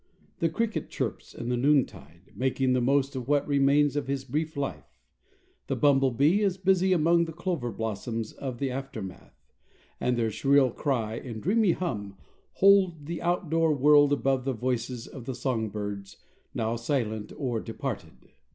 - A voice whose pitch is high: No, low, 135 Hz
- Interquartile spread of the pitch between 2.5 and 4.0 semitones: No, average, 4.6 semitones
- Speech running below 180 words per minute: Yes, average, 160 wpm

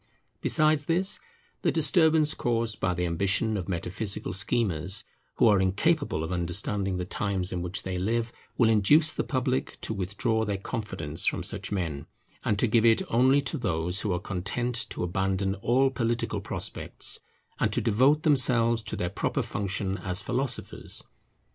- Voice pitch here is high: No, low, 105 Hz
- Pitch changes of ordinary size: Yes, average, 4.8 semitones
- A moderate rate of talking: Yes, average, 160 wpm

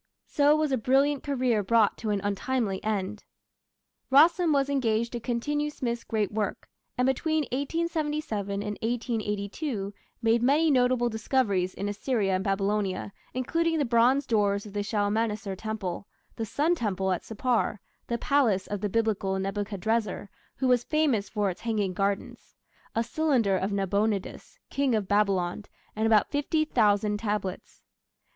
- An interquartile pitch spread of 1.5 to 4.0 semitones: No, average, 4.5 semitones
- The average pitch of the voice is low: No, high, 220 Hz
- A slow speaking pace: No, average, 145 wpm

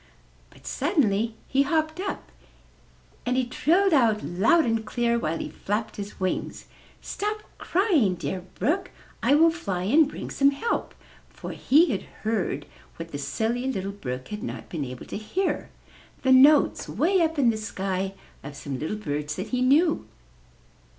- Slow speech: No, average, 165 wpm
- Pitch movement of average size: No, wide, 8.2 semitones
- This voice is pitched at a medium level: No, high, 230 Hz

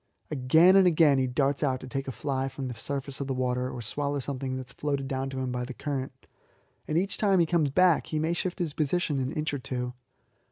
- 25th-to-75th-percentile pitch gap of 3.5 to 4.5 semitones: No, average, 3.0 semitones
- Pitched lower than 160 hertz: Yes, low, 135 Hz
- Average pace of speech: No, fast, 250 wpm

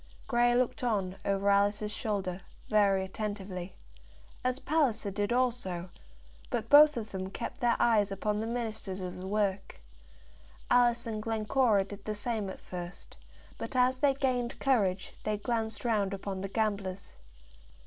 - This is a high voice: Yes, high, 210 Hz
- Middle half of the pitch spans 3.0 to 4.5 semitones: Yes, average, 3.5 semitones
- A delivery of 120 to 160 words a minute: Yes, average, 150 wpm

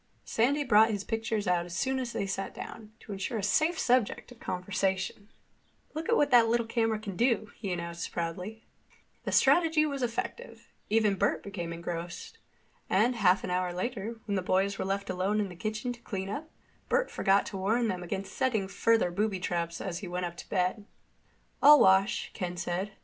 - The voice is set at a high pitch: Yes, high, 205 Hz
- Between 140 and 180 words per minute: No, average, 195 wpm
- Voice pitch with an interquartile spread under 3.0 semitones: No, average, 4.0 semitones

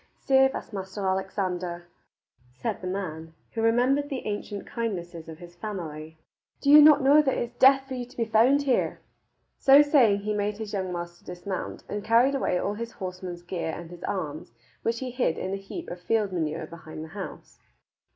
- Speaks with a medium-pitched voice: No, high, 200 Hz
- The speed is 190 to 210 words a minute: Yes, average, 195 wpm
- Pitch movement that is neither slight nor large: No, wide, 5.8 semitones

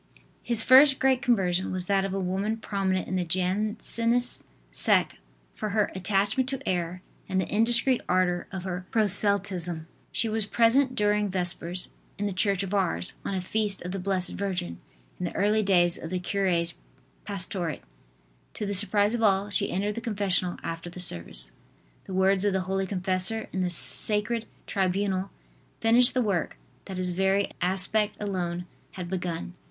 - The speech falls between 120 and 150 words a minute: No, average, 170 wpm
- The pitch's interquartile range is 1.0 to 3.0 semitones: Yes, narrow, 2.6 semitones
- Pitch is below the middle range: No, high, 195 Hz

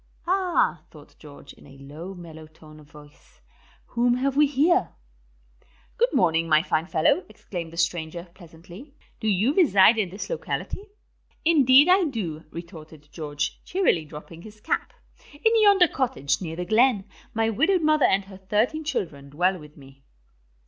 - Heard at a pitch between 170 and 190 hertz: Yes, medium, 185 Hz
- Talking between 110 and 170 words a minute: Yes, average, 155 wpm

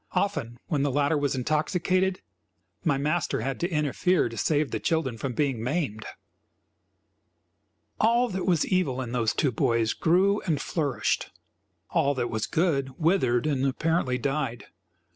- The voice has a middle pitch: Yes, medium, 145 Hz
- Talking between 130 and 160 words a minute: Yes, average, 145 wpm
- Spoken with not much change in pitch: No, average, 5.1 semitones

